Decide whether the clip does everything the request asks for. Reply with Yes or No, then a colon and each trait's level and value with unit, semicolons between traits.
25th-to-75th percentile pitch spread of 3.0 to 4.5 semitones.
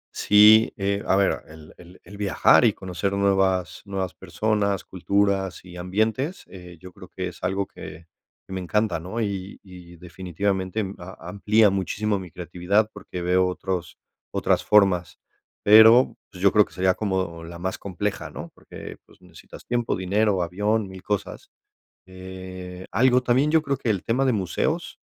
No: narrow, 2.4 semitones